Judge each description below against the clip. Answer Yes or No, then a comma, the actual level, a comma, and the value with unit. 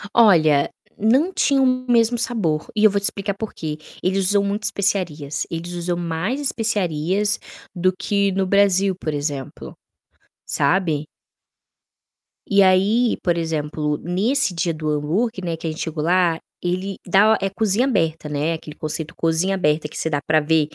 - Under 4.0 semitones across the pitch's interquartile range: No, average, 4.3 semitones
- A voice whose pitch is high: No, medium, 180 Hz